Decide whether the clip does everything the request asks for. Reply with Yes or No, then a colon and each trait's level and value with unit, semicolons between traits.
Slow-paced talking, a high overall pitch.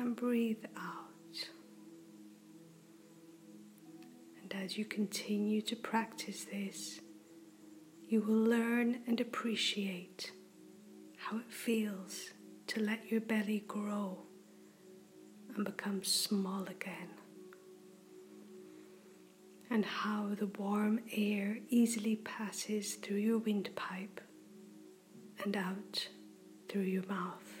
Yes: slow, 90 wpm; high, 200 Hz